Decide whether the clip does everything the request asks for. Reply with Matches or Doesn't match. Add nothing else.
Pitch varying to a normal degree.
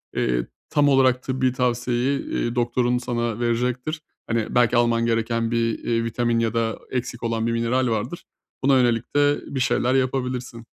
Doesn't match